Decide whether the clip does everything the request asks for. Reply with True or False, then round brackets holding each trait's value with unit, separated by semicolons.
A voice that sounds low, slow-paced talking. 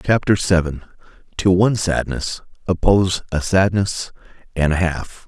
True (90 Hz; 115 wpm)